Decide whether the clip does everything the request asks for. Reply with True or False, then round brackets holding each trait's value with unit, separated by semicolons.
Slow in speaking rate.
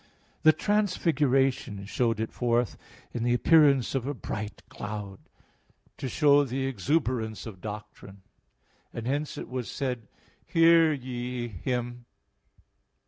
True (125 wpm)